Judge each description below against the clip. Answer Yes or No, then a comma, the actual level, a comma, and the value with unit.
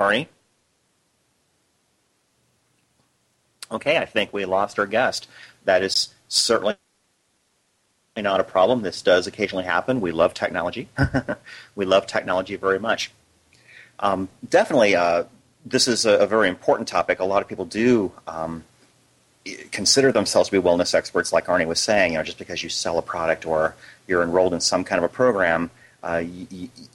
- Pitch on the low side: Yes, very low, 95 Hz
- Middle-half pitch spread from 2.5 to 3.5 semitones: No, average, 5.1 semitones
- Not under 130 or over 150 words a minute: No, average, 160 wpm